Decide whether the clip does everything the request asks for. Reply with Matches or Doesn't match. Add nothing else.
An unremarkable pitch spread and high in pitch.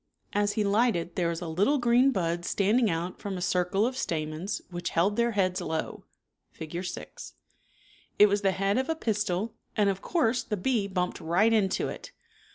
Matches